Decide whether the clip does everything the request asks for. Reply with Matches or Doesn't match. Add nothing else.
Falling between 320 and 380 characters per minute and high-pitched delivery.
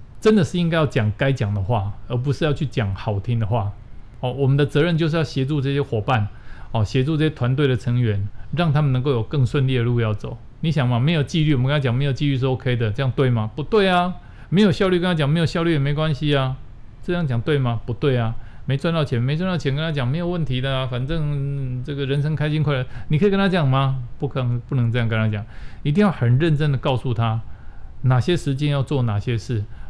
Doesn't match